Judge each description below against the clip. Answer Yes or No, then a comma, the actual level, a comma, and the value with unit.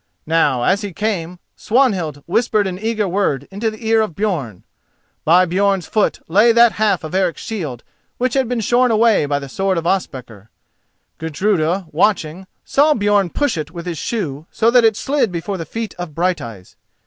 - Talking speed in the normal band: Yes, average, 180 wpm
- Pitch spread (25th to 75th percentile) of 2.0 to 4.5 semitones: No, average, 5.2 semitones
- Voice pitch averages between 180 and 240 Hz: Yes, high, 190 Hz